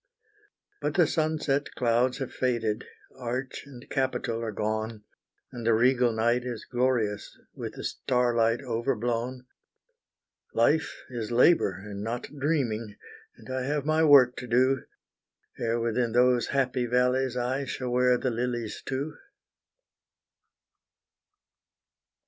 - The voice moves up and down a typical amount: No, narrow, 2.1 semitones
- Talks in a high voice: No, low, 125 Hz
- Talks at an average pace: No, slow, 120 wpm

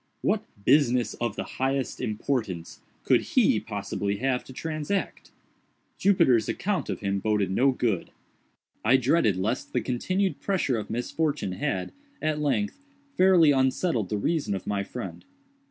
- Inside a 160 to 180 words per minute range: No, average, 140 wpm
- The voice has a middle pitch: No, low, 125 Hz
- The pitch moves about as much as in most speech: No, wide, 6.8 semitones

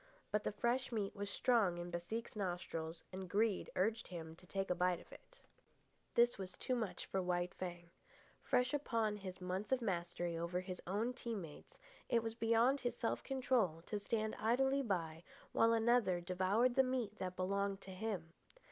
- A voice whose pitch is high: Yes, high, 200 Hz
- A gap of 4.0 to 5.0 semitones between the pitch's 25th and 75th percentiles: Yes, average, 4.4 semitones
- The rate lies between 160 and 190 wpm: Yes, average, 180 wpm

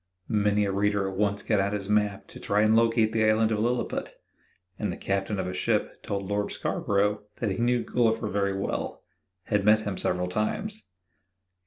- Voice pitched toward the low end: Yes, low, 105 Hz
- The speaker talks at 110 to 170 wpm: No, average, 190 wpm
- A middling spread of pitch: No, narrow, 1.7 semitones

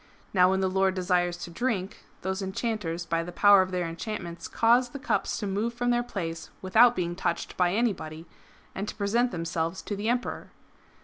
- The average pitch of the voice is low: No, high, 190 Hz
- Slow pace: No, average, 195 wpm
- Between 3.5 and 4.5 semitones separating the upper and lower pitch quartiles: Yes, average, 4.2 semitones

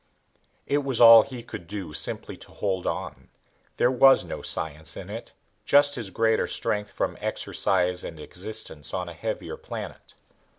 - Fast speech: No, average, 160 wpm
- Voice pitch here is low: Yes, low, 105 Hz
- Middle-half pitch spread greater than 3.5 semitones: Yes, average, 4.9 semitones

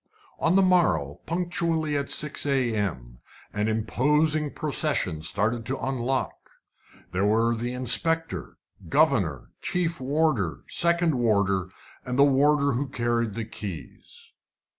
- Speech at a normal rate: No, slow, 120 wpm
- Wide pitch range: Yes, wide, 6.2 semitones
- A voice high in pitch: No, low, 130 Hz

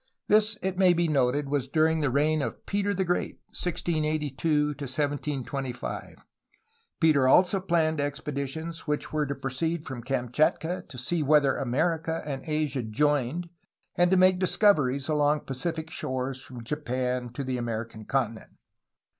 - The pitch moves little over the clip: No, average, 3.7 semitones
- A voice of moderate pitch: Yes, medium, 150 Hz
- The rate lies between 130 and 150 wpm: Yes, average, 145 wpm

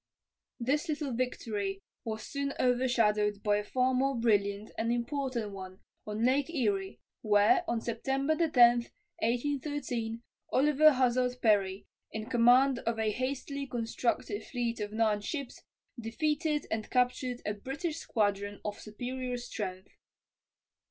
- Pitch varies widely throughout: No, average, 3.9 semitones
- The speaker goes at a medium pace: No, slow, 125 wpm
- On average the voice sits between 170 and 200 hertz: No, high, 240 Hz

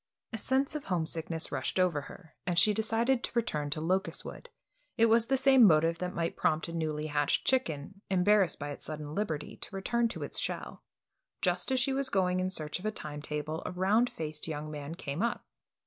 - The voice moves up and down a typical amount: No, wide, 6.5 semitones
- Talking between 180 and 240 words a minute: Yes, fast, 205 wpm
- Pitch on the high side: No, medium, 180 Hz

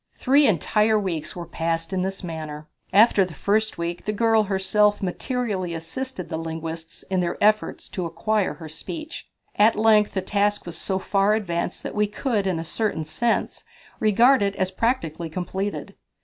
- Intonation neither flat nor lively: Yes, average, 4.1 semitones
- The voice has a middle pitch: No, high, 195 Hz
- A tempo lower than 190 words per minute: Yes, average, 170 wpm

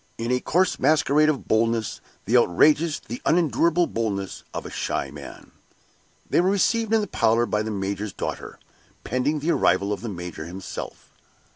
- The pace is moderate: Yes, average, 165 wpm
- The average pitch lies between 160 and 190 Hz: No, low, 120 Hz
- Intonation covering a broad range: Yes, wide, 7.1 semitones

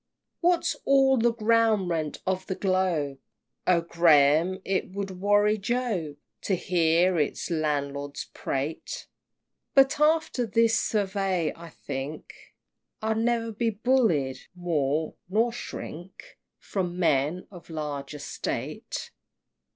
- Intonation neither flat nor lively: No, wide, 6.1 semitones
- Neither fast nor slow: No, slow, 115 wpm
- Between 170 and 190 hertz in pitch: Yes, medium, 185 Hz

